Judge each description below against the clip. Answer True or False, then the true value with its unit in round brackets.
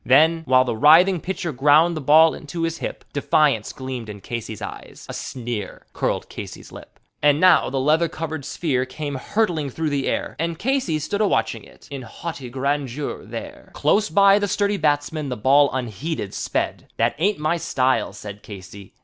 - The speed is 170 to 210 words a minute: True (180 wpm)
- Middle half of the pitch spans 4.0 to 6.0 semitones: True (4.4 semitones)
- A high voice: False (145 Hz)